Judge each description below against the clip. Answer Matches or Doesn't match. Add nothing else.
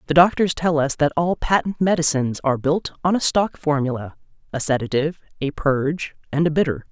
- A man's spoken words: Doesn't match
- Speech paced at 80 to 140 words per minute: Doesn't match